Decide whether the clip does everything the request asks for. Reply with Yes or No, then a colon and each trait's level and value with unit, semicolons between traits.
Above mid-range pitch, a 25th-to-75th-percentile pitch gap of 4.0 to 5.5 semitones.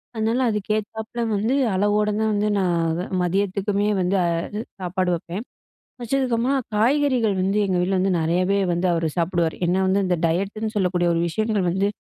No: high, 200 Hz; average, 3.3 semitones